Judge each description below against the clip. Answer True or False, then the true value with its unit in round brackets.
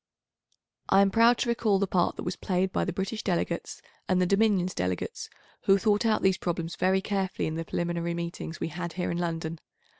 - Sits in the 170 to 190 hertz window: True (185 Hz)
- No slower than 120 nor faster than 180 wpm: False (205 wpm)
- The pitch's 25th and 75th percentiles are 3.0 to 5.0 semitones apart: False (2.5 semitones)